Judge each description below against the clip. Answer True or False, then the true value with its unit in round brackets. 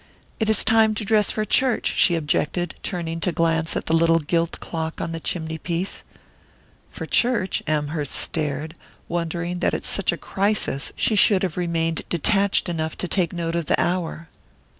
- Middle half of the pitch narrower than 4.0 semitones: True (2.9 semitones)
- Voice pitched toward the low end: False (170 Hz)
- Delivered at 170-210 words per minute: True (175 wpm)